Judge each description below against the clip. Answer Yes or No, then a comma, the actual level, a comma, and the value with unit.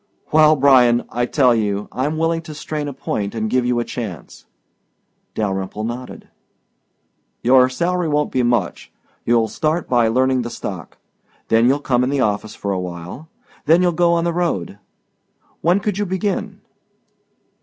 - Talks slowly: No, average, 165 wpm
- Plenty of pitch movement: Yes, wide, 5.9 semitones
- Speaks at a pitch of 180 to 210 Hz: No, low, 130 Hz